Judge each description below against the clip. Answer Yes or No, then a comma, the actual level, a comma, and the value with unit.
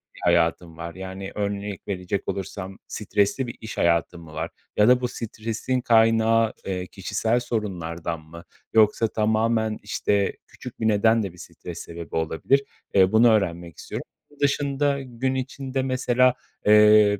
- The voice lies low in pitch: Yes, low, 105 Hz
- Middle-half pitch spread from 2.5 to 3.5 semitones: No, average, 4.1 semitones